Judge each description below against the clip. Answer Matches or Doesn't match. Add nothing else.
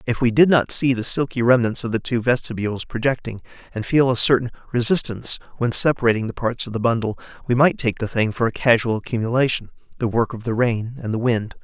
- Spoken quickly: Matches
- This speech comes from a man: Matches